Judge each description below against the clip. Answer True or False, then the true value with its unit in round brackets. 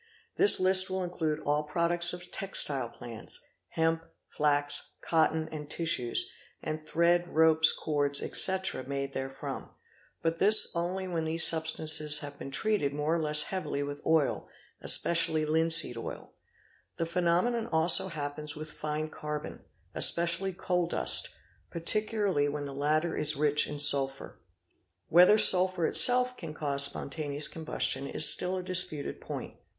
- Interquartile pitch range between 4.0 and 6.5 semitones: False (3.0 semitones)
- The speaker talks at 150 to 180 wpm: False (140 wpm)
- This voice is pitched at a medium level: True (160 Hz)